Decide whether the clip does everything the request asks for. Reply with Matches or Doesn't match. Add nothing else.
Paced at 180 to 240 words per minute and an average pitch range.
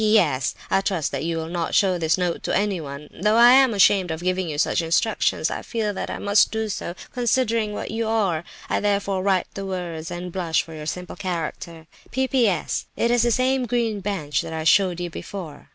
Matches